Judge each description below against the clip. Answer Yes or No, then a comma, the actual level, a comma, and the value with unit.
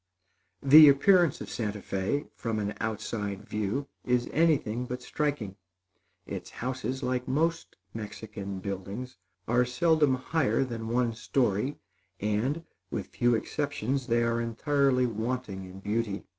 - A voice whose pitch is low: Yes, low, 120 Hz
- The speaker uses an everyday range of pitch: Yes, average, 4.3 semitones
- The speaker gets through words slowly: Yes, slow, 130 wpm